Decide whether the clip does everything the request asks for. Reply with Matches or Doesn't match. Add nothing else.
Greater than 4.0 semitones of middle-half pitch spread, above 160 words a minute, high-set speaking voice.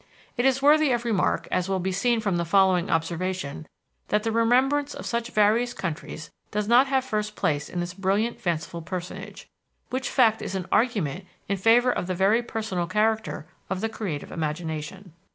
Matches